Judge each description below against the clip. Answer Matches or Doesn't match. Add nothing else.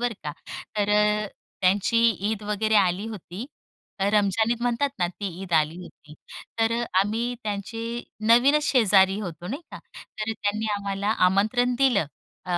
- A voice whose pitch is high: Matches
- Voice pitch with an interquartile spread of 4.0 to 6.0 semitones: Doesn't match